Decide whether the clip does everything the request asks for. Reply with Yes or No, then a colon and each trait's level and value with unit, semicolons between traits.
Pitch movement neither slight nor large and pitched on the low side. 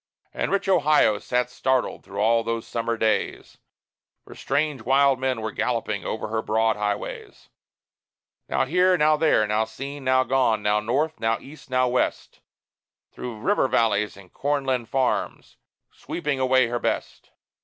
Yes: average, 3.8 semitones; low, 125 Hz